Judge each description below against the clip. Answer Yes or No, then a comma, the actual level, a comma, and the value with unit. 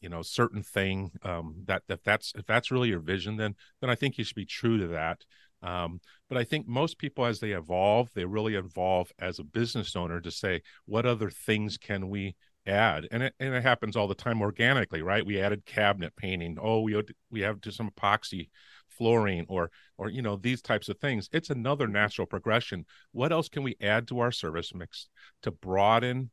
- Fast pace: Yes, fast, 210 wpm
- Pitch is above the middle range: No, low, 105 Hz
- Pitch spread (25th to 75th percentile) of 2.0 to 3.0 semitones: No, average, 3.8 semitones